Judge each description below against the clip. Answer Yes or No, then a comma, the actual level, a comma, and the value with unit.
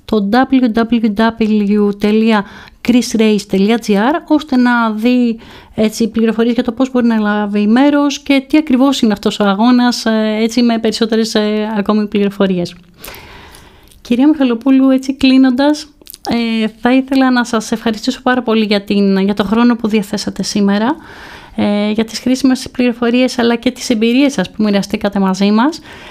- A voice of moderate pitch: No, high, 230 Hz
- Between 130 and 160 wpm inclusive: Yes, average, 135 wpm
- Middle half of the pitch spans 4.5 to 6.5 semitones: No, average, 3.1 semitones